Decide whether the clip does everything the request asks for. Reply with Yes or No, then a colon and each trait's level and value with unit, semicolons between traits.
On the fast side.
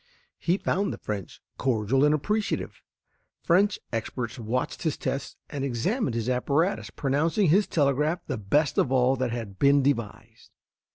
No: average, 150 wpm